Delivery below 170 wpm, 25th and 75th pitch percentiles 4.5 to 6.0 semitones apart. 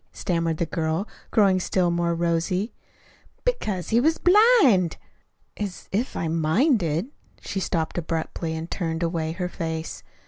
No: average, 140 wpm; average, 3.9 semitones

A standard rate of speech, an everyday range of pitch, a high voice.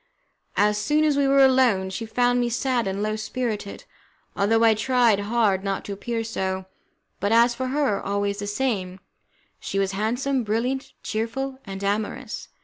Yes: average, 165 wpm; average, 3.9 semitones; high, 225 Hz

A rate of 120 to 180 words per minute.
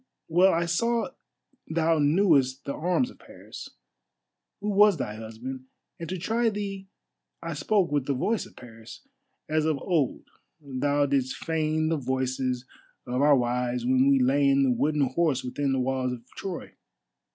Yes: average, 165 wpm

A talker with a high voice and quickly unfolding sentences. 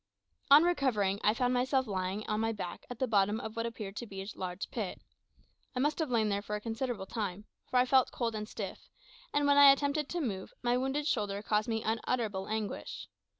Yes: high, 225 Hz; fast, 215 wpm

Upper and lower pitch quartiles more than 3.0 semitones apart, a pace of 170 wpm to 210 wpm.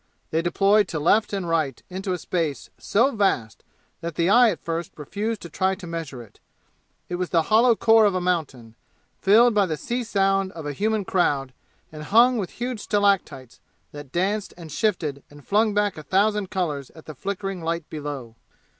Yes: average, 5.0 semitones; average, 190 wpm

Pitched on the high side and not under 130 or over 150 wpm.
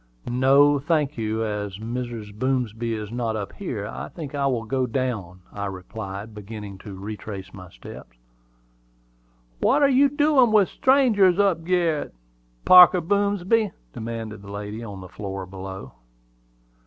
No: low, 115 Hz; average, 145 wpm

